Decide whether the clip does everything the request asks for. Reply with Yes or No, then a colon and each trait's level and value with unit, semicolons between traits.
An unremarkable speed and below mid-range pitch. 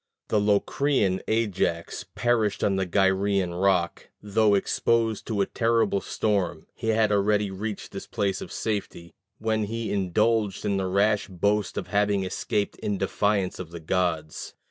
Yes: average, 150 wpm; low, 100 Hz